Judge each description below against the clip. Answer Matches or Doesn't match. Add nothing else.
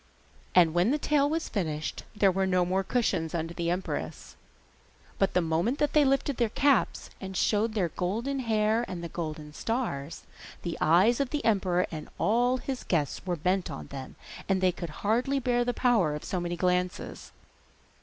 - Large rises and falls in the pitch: Matches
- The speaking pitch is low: Doesn't match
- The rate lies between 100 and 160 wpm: Doesn't match